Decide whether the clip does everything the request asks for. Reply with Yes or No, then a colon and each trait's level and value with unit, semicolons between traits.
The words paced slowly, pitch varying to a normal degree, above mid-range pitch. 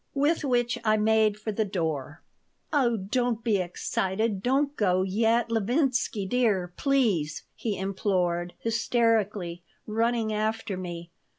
Yes: slow, 120 wpm; average, 3.9 semitones; high, 215 Hz